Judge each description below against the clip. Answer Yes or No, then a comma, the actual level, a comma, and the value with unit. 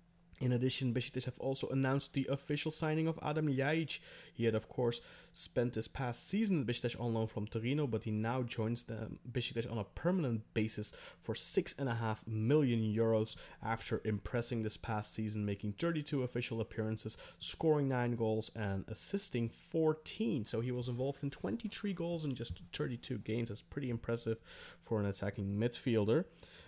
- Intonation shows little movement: No, average, 4.1 semitones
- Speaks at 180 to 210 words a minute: No, average, 165 wpm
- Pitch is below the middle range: Yes, low, 120 Hz